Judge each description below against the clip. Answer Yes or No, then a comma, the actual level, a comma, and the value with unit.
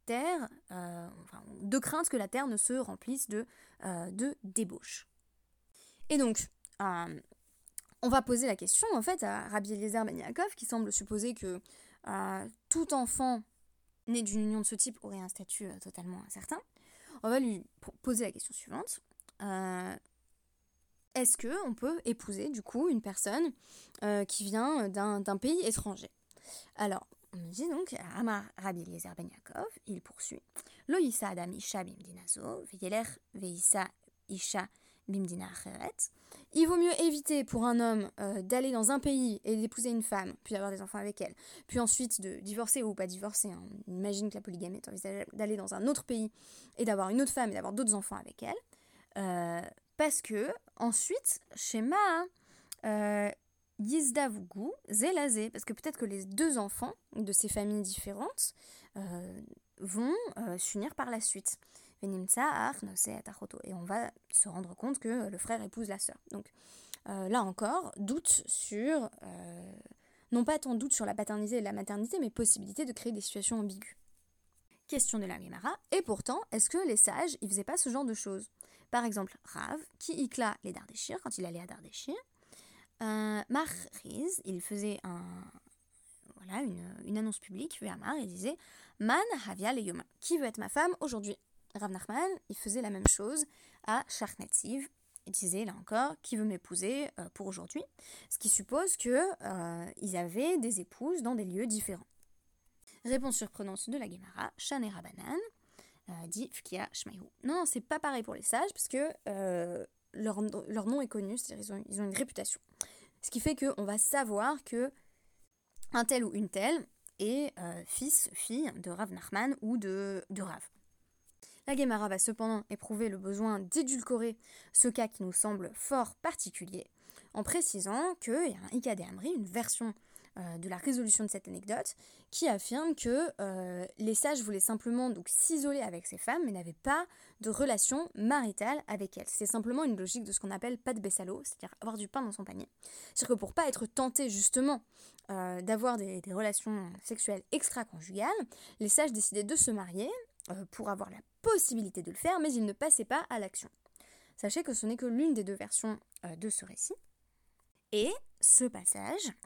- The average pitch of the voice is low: No, high, 220 Hz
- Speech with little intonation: No, average, 5.1 semitones